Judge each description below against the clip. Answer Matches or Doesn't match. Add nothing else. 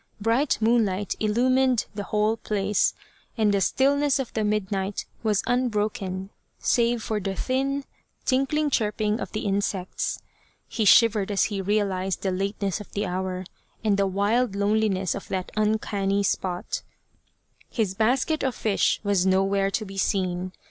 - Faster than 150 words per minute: Doesn't match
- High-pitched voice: Matches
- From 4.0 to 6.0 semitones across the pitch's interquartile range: Doesn't match